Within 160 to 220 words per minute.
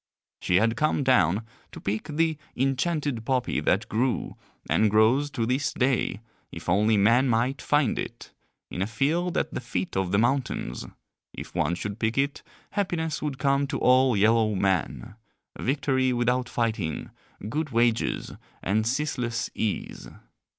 No: average, 150 wpm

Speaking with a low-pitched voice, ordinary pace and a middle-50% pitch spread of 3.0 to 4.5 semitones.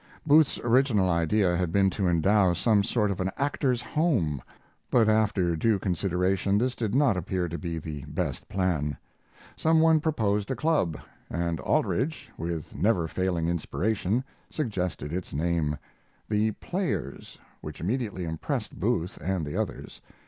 No: very low, 95 Hz; average, 145 wpm; average, 5.2 semitones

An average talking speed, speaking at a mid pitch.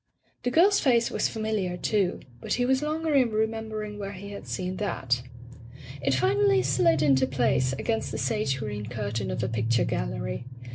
Yes: average, 175 wpm; medium, 180 Hz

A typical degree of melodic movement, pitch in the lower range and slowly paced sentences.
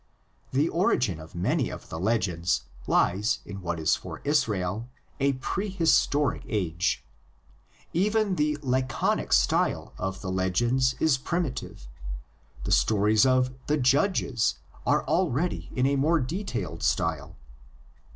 No: wide, 8.1 semitones; low, 125 Hz; slow, 120 wpm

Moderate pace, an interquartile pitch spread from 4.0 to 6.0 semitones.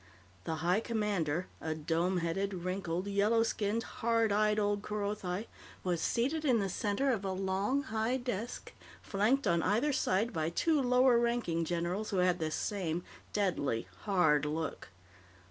Yes: average, 150 wpm; average, 4.6 semitones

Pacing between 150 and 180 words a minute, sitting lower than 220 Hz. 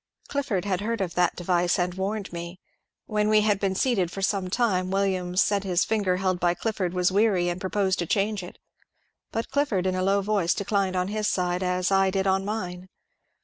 No: fast, 205 wpm; high, 190 Hz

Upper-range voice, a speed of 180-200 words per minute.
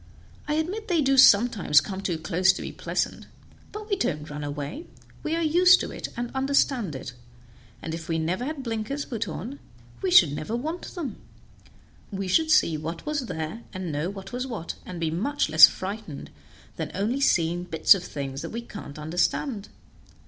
Yes: high, 200 Hz; average, 190 wpm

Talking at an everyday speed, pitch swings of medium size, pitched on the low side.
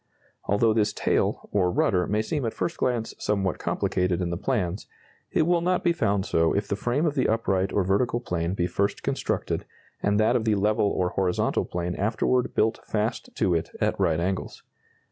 Yes: average, 195 wpm; average, 4.1 semitones; low, 105 Hz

